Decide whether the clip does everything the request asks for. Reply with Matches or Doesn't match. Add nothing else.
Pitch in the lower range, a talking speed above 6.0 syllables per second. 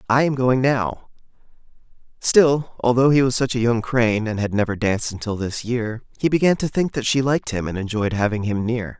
Doesn't match